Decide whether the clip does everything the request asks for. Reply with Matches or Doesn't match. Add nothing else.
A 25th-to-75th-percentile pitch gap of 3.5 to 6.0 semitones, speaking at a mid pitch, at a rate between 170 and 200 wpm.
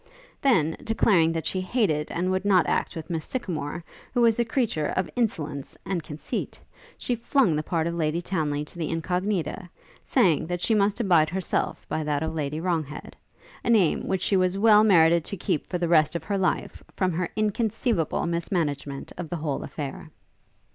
Matches